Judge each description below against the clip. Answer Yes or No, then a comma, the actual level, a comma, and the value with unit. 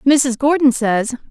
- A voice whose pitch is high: Yes, very high, 255 Hz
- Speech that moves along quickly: No, average, 140 wpm